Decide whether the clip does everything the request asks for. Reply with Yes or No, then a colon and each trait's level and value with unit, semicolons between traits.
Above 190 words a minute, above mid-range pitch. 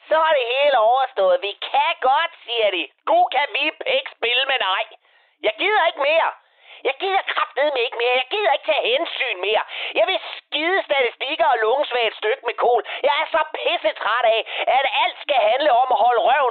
Yes: average, 205 wpm; very high, 310 Hz